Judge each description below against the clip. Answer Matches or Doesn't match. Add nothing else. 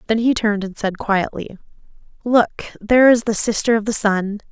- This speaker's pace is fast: Doesn't match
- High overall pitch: Matches